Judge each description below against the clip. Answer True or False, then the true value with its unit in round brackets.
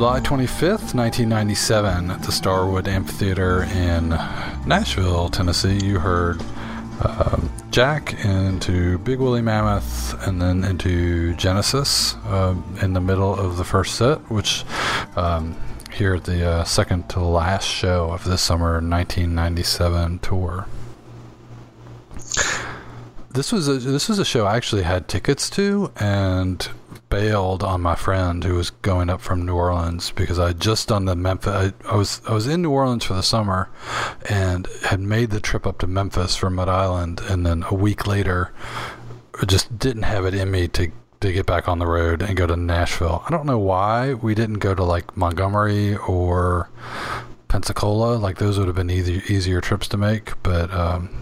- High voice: False (95 Hz)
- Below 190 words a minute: True (170 wpm)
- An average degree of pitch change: True (3.8 semitones)